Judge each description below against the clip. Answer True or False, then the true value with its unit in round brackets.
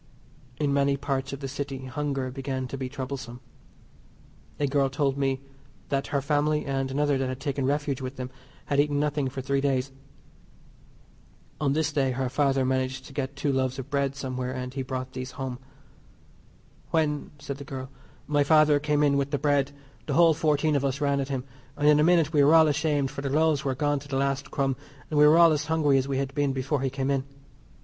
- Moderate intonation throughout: False (1.7 semitones)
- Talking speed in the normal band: False (215 wpm)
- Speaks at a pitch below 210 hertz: True (140 Hz)